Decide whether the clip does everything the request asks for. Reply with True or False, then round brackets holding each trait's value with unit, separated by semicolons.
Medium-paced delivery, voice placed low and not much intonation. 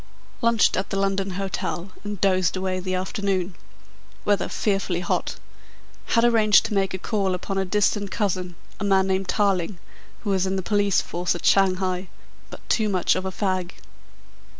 False (170 wpm; 195 Hz; 1.6 semitones)